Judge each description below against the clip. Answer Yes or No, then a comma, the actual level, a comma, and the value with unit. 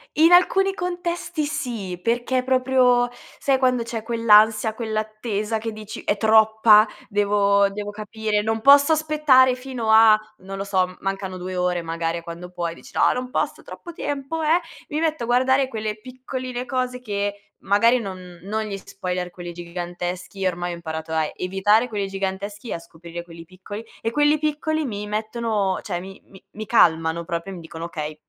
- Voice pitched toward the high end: Yes, high, 215 Hz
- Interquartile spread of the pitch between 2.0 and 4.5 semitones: No, average, 5.3 semitones